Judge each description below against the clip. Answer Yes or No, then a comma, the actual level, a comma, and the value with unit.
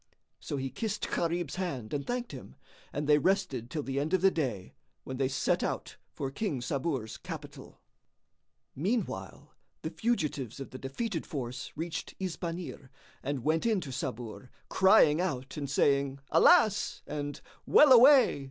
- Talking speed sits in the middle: Yes, average, 150 wpm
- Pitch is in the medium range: Yes, medium, 150 Hz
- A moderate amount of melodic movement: No, wide, 5.9 semitones